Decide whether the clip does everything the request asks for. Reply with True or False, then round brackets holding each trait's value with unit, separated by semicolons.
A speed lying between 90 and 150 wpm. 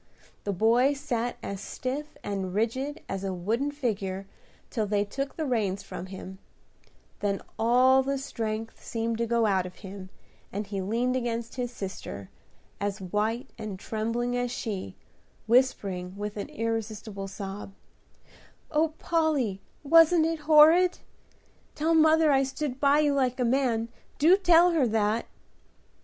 True (145 wpm)